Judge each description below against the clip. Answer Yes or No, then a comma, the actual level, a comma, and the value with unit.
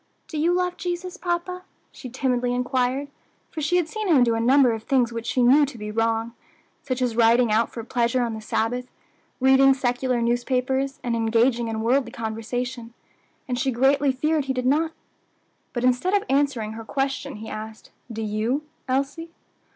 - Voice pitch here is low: No, very high, 250 Hz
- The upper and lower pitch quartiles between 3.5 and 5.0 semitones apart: No, average, 3.1 semitones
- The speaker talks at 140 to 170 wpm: No, average, 180 wpm